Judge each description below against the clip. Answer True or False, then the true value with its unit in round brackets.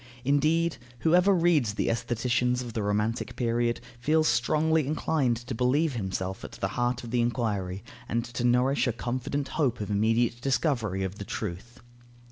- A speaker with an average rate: True (160 wpm)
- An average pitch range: True (3.8 semitones)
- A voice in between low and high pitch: False (120 Hz)